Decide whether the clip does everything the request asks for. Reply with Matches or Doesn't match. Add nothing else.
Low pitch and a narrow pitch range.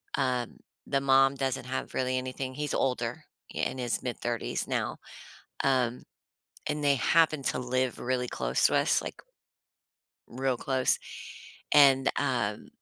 Matches